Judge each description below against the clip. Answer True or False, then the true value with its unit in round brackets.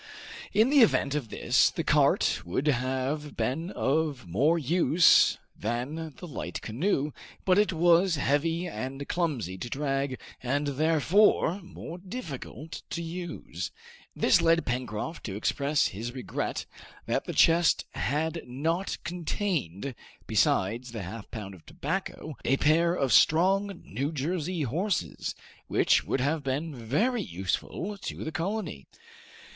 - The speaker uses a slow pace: True (130 wpm)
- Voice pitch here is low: False (150 Hz)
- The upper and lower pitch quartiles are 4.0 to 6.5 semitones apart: True (5.1 semitones)